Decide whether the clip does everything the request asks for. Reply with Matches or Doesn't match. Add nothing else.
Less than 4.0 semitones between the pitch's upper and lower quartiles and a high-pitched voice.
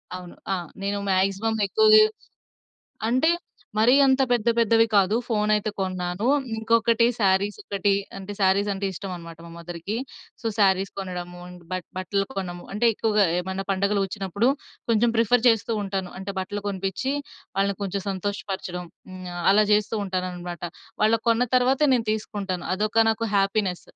Matches